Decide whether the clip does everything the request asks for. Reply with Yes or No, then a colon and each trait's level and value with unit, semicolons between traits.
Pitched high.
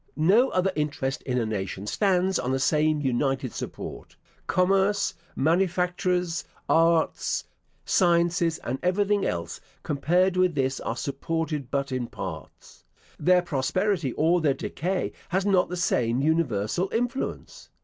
No: medium, 165 Hz